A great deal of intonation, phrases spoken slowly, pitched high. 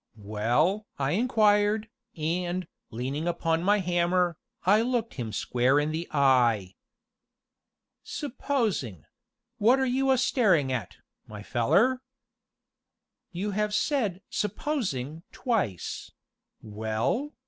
No: wide, 9.0 semitones; slow, 105 wpm; medium, 175 Hz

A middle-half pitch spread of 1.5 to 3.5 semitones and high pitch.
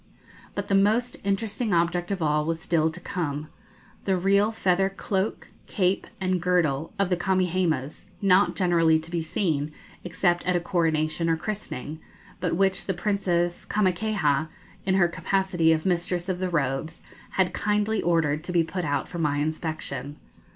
No: average, 3.1 semitones; medium, 175 Hz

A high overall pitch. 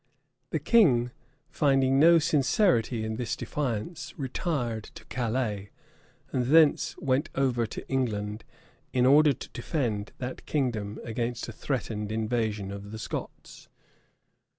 No: low, 125 Hz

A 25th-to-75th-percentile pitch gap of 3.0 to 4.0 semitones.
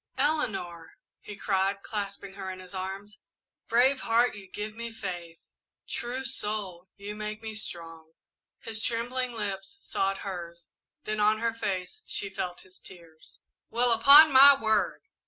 Yes: average, 3.7 semitones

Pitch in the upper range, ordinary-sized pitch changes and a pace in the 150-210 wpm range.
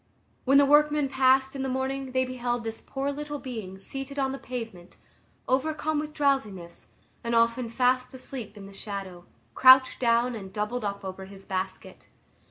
Yes: very high, 250 Hz; average, 4.6 semitones; average, 170 wpm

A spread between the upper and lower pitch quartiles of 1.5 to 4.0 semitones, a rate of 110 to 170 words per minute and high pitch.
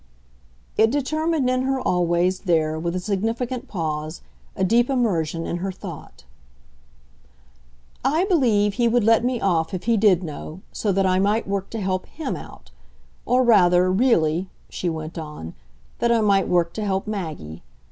No: wide, 5.4 semitones; average, 165 wpm; high, 195 Hz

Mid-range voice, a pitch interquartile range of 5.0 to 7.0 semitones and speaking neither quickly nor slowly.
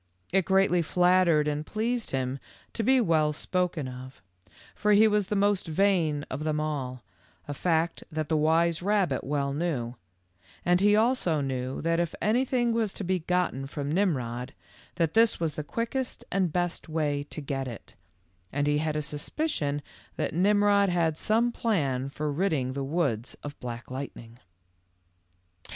Yes: medium, 160 Hz; wide, 5.5 semitones; average, 160 wpm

